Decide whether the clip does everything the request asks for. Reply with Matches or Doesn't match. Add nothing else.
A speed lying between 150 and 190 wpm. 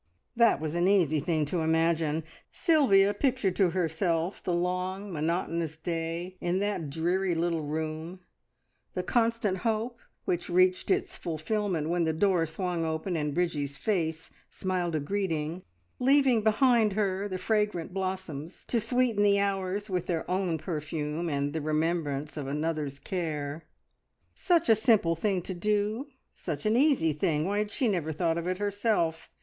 Matches